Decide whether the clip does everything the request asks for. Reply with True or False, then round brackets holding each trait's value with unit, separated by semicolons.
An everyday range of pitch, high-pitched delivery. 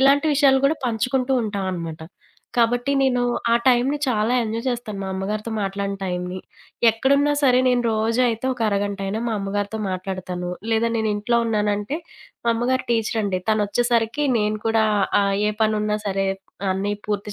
True (3.4 semitones; 220 Hz)